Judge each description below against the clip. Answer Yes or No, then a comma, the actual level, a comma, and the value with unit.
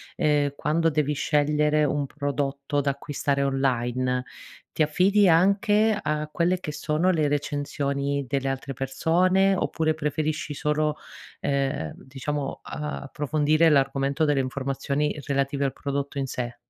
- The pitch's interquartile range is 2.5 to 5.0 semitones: No, narrow, 1.9 semitones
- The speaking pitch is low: No, medium, 145 Hz